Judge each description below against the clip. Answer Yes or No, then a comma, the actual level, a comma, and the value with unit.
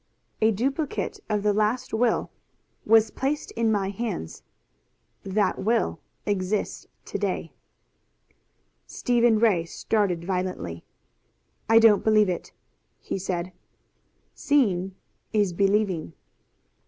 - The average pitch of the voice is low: No, high, 210 Hz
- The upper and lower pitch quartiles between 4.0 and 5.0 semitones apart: No, average, 3.2 semitones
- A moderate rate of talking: No, slow, 105 wpm